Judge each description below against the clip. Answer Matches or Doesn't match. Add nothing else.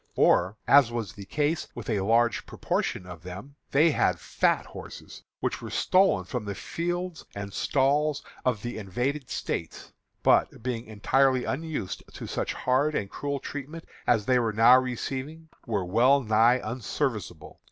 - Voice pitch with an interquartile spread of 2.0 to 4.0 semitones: Doesn't match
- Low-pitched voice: Matches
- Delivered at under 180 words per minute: Matches